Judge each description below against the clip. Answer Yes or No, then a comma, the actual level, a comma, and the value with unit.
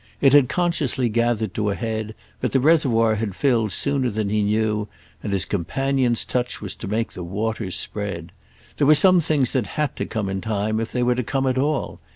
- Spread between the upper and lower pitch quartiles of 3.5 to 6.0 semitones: Yes, average, 4.2 semitones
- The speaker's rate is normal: No, fast, 210 wpm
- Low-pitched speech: Yes, low, 115 Hz